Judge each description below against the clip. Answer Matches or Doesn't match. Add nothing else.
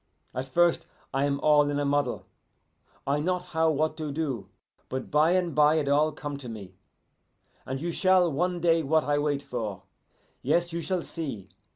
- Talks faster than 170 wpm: Matches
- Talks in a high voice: Doesn't match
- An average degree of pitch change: Matches